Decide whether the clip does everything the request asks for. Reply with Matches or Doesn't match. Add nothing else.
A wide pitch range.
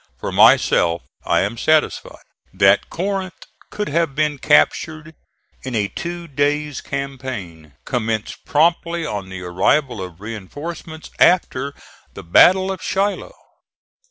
Matches